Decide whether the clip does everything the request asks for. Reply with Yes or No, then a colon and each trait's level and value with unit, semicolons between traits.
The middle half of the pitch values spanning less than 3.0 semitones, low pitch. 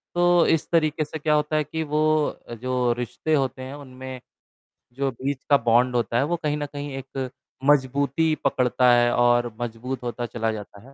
No: average, 3.4 semitones; low, 130 Hz